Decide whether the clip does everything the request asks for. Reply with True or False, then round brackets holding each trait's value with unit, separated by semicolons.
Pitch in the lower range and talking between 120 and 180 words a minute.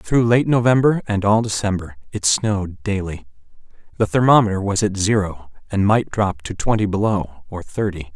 True (100 Hz; 160 wpm)